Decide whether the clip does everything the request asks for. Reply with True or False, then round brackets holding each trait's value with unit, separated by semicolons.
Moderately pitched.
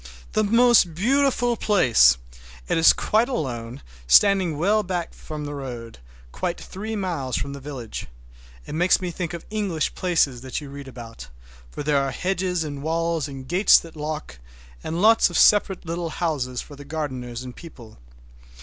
True (160 Hz)